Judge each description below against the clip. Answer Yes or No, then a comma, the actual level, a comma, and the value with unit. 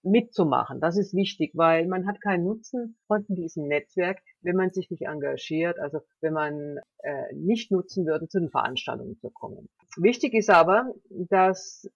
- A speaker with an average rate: Yes, average, 165 wpm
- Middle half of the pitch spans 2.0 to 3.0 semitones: No, average, 3.7 semitones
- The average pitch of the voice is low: No, medium, 185 Hz